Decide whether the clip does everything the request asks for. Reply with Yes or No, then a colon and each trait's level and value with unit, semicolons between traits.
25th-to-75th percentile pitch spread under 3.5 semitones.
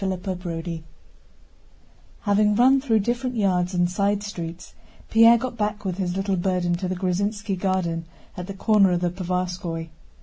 Yes: average, 2.7 semitones